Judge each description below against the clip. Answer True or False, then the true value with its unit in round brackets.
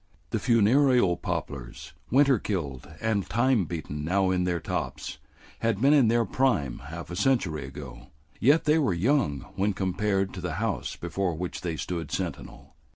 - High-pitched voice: False (95 Hz)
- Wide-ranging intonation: True (6.2 semitones)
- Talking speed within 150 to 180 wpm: True (160 wpm)